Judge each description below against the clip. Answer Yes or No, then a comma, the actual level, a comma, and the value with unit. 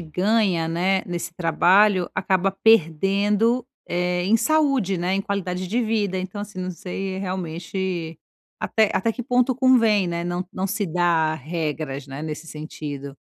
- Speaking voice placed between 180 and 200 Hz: Yes, medium, 185 Hz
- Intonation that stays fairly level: No, average, 3.6 semitones